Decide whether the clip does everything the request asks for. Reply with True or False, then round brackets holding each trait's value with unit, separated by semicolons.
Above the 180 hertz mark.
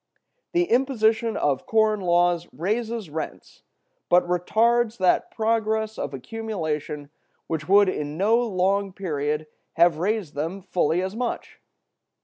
True (190 Hz)